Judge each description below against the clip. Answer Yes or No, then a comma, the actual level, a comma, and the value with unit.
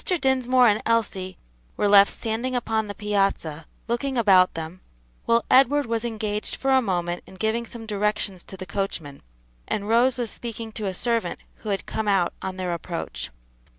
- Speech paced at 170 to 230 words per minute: Yes, average, 175 wpm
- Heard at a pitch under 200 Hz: No, high, 210 Hz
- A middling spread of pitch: Yes, average, 3.8 semitones